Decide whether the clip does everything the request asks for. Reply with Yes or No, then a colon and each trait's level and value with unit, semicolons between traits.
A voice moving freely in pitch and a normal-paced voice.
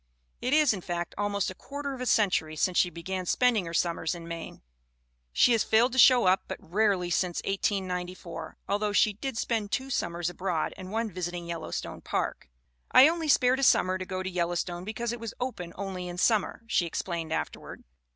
No: average, 4.6 semitones; average, 195 wpm